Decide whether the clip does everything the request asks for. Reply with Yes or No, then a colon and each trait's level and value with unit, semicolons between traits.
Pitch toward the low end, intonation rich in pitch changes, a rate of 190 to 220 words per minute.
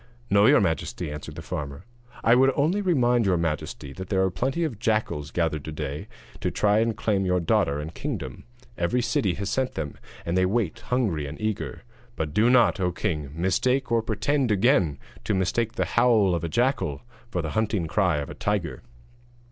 Yes: low, 100 Hz; wide, 6.3 semitones; average, 195 wpm